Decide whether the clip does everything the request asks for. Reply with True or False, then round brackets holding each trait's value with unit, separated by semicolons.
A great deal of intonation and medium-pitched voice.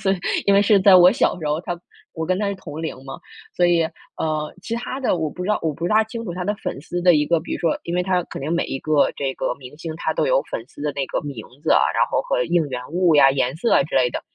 False (4.1 semitones; 170 Hz)